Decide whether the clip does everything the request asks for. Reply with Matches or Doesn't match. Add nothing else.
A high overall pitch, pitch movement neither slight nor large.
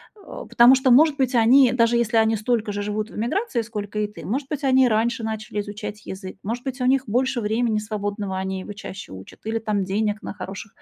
Matches